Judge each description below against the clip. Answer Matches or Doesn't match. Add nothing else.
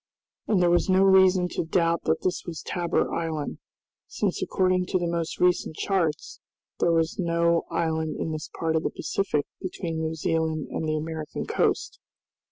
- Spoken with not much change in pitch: Matches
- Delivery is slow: Doesn't match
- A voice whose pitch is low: Doesn't match